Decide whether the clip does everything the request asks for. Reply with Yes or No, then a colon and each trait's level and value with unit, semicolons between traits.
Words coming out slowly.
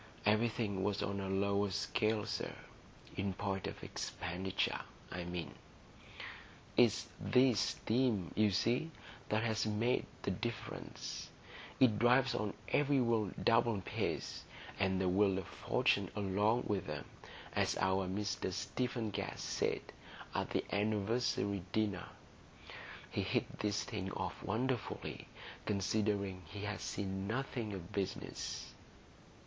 Yes: slow, 120 wpm